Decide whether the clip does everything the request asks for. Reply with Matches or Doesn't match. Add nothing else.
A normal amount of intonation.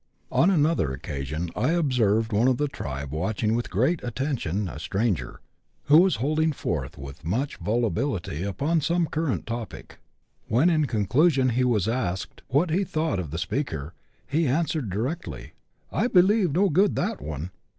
Doesn't match